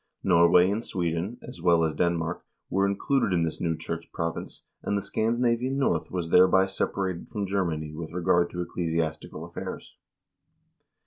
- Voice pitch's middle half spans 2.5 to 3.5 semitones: Yes, average, 2.9 semitones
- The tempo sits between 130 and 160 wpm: Yes, average, 150 wpm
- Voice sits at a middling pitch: No, very low, 90 Hz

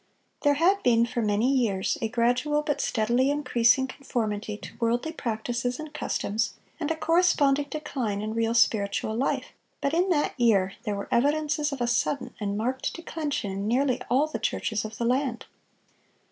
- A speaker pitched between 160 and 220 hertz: No, high, 245 Hz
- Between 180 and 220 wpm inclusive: No, average, 170 wpm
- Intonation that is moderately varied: Yes, average, 4.7 semitones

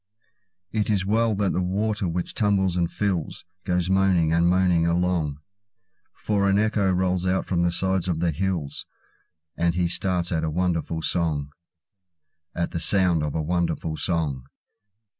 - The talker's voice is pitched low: Yes, very low, 90 Hz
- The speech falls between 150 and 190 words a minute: No, average, 140 wpm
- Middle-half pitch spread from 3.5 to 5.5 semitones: No, narrow, 2.5 semitones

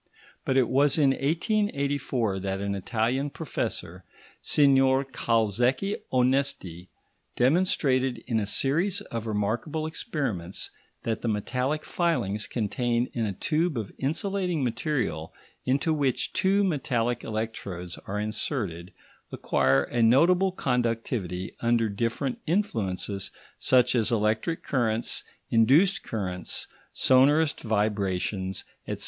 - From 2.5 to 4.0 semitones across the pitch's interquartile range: No, average, 5.3 semitones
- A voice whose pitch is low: Yes, low, 120 Hz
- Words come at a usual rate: No, slow, 110 wpm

